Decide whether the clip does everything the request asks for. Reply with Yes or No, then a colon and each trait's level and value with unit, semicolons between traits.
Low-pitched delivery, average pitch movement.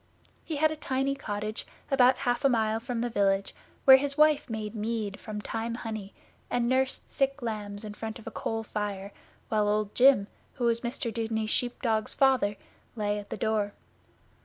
No: high, 225 Hz; average, 3.4 semitones